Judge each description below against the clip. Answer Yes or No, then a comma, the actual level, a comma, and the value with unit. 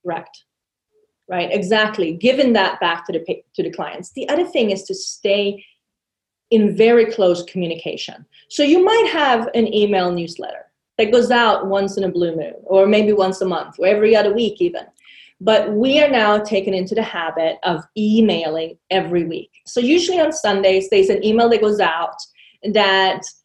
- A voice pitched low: No, high, 210 Hz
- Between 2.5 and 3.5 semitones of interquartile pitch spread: No, average, 4.2 semitones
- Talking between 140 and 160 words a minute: No, average, 180 wpm